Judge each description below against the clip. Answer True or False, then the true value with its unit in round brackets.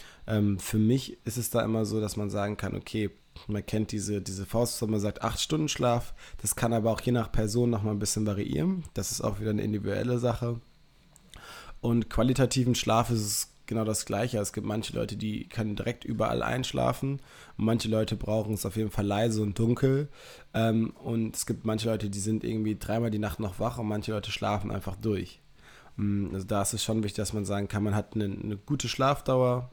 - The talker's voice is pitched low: True (110 Hz)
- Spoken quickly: True (205 wpm)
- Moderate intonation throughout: False (2.1 semitones)